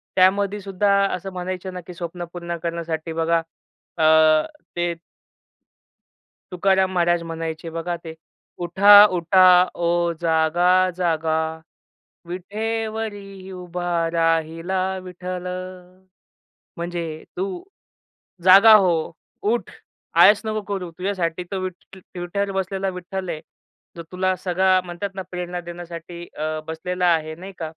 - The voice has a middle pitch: Yes, medium, 180 Hz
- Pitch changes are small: Yes, narrow, 2.0 semitones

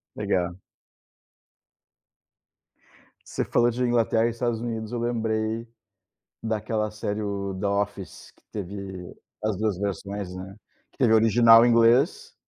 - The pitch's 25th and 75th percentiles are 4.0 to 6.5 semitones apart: No, narrow, 2.6 semitones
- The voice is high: No, low, 110 Hz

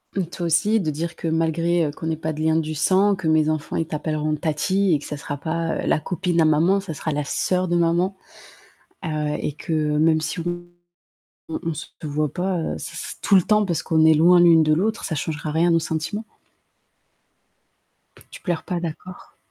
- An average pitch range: No, narrow, 2.2 semitones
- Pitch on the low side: No, medium, 165 Hz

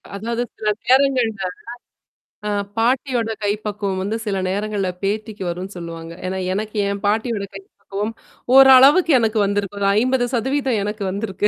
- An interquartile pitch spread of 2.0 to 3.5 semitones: Yes, average, 2.9 semitones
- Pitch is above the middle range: Yes, high, 210 Hz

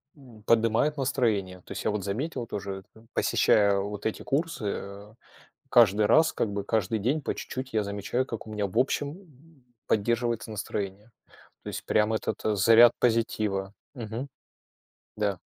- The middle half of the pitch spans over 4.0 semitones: No, average, 3.5 semitones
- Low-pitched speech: Yes, low, 110 Hz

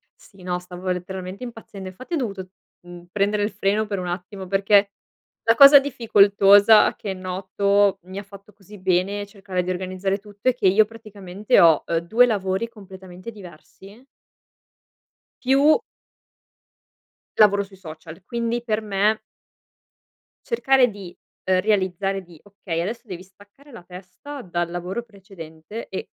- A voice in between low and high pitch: No, high, 195 Hz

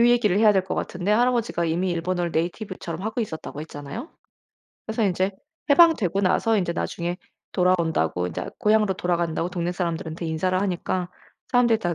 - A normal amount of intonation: Yes, average, 3.9 semitones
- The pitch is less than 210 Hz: Yes, medium, 185 Hz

